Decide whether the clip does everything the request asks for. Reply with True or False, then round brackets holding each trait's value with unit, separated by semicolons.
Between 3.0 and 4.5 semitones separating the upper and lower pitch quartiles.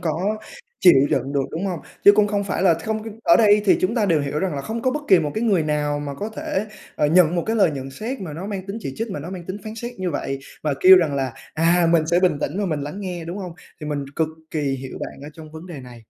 False (5.3 semitones)